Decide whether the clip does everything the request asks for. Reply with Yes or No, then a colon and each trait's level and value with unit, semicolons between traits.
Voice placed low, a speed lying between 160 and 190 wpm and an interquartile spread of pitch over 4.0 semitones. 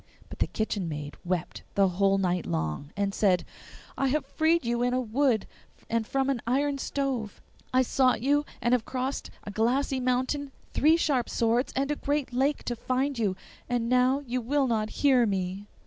No: high, 245 Hz; average, 185 wpm; average, 4.7 semitones